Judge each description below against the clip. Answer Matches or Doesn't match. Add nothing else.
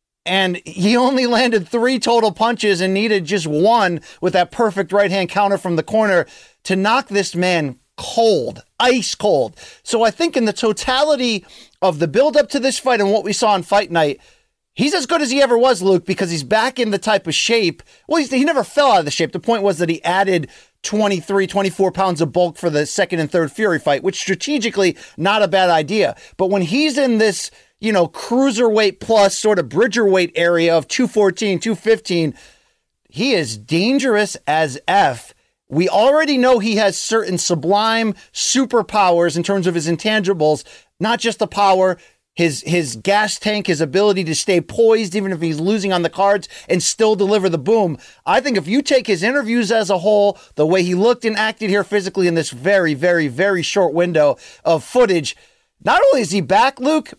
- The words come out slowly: Doesn't match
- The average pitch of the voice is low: Doesn't match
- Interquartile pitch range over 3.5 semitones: Matches